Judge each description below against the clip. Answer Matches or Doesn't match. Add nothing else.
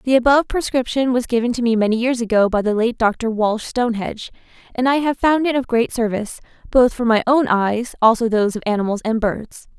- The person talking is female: Matches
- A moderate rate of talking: Doesn't match